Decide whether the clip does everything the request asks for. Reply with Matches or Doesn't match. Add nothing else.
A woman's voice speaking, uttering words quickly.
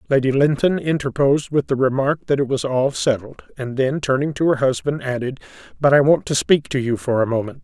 Doesn't match